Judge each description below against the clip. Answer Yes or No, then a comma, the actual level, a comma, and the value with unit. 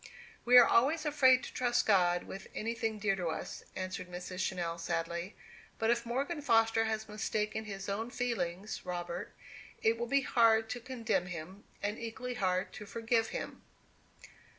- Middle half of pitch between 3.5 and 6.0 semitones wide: Yes, average, 4.2 semitones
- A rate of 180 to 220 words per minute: No, average, 160 wpm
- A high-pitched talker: Yes, high, 220 Hz